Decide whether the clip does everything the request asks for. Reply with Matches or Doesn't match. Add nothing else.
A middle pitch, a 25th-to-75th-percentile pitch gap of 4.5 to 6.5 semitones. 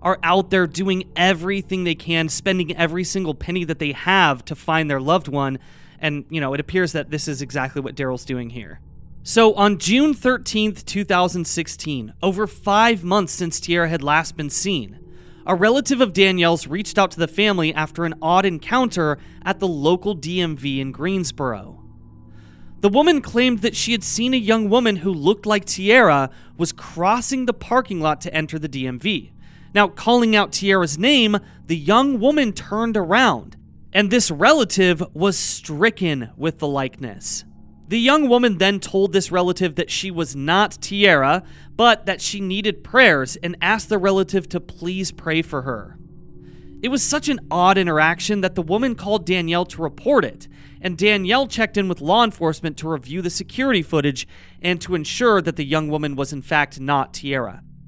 Matches